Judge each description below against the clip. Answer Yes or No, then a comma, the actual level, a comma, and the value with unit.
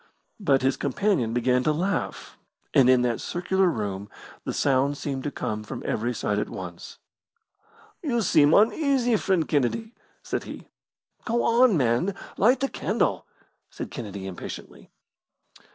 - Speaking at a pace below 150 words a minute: Yes, average, 140 wpm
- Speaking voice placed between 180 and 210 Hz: No, medium, 140 Hz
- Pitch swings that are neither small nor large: No, wide, 8.9 semitones